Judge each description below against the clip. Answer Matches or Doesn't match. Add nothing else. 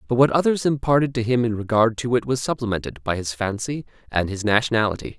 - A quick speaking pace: Matches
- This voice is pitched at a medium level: Doesn't match